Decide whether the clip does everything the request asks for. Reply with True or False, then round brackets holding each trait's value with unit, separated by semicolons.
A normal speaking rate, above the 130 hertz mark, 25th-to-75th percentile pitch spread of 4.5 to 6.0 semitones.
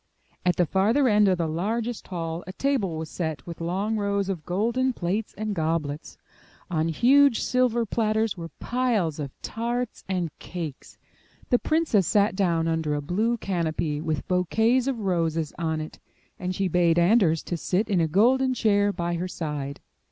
True (170 wpm; 185 Hz; 5.2 semitones)